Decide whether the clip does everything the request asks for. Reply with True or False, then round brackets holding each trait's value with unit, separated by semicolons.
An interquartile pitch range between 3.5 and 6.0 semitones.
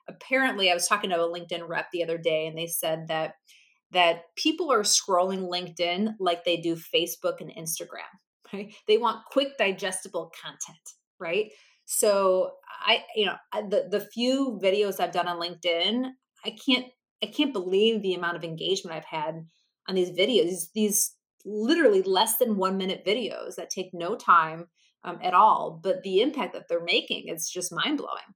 True (4.2 semitones)